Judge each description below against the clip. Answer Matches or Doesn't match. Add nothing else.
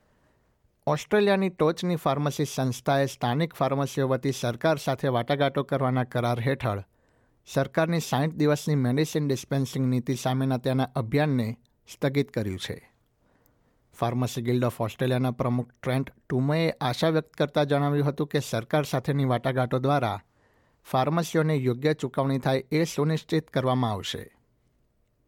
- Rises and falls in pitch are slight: Doesn't match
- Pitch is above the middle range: Doesn't match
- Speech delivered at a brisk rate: Doesn't match